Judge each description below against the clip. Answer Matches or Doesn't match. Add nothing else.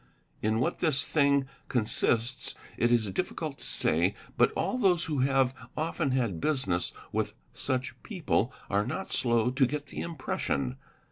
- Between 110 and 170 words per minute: Matches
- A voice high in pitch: Doesn't match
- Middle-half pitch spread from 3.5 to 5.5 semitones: Matches